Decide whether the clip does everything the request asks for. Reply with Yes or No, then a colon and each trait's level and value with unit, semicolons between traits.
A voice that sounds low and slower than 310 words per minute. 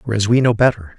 Yes: low, 110 Hz; fast, 245 wpm